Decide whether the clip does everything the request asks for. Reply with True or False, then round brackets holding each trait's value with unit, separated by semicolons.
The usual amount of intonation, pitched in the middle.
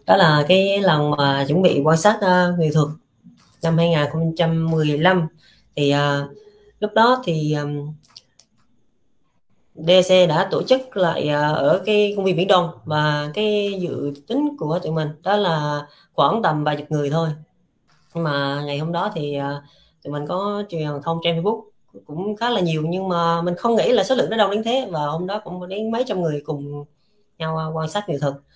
True (4.7 semitones; 165 Hz)